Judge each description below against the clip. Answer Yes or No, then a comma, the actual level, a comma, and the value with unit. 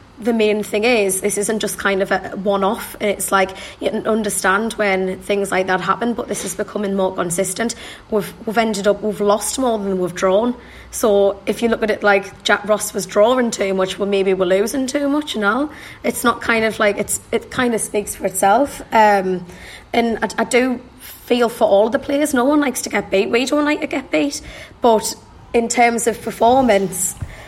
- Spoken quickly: Yes, fast, 210 wpm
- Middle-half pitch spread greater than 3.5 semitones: No, average, 3.0 semitones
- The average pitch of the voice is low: No, high, 210 Hz